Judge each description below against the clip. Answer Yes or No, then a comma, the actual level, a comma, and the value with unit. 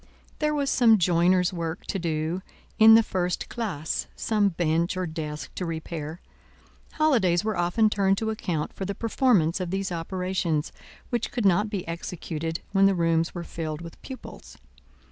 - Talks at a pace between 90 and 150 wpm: No, average, 165 wpm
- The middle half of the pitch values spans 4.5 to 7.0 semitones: No, average, 3.9 semitones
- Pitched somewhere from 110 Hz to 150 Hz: No, medium, 180 Hz